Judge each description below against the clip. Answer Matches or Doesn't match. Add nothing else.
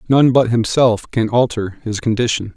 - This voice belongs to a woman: Doesn't match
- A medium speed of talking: Matches